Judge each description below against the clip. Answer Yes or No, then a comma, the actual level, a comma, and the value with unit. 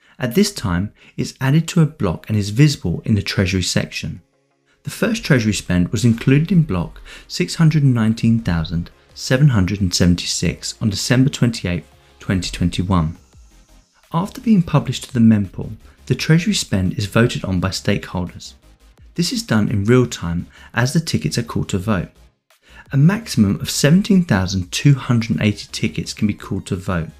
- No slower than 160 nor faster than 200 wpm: No, average, 145 wpm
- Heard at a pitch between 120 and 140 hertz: No, low, 110 Hz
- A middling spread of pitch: No, wide, 7.9 semitones